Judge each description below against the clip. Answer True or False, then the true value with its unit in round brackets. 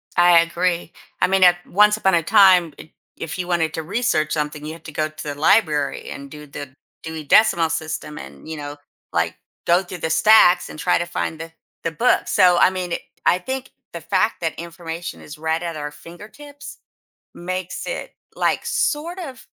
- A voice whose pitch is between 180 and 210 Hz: False (170 Hz)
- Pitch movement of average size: True (3.0 semitones)